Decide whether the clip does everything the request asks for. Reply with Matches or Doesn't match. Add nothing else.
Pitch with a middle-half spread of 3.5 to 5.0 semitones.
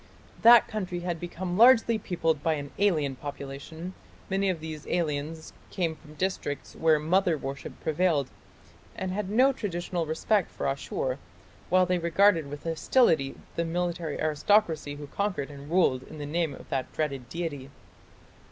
Matches